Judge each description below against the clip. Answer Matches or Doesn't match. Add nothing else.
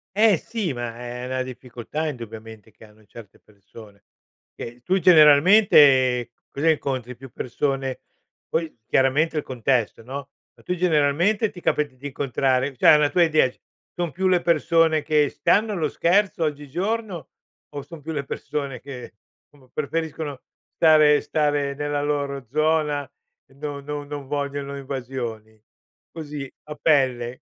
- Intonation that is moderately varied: Matches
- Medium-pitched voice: Matches